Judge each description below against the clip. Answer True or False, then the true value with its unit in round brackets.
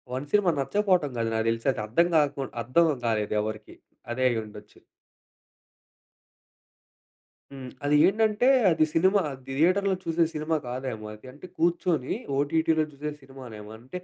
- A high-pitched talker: False (145 Hz)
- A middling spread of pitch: False (6.3 semitones)